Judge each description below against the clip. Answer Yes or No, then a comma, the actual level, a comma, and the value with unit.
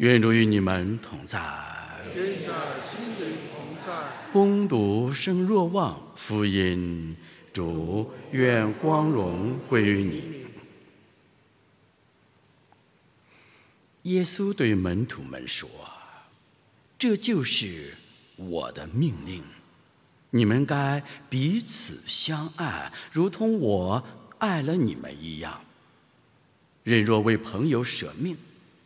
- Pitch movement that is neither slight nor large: No, wide, 8.2 semitones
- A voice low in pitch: Yes, low, 125 Hz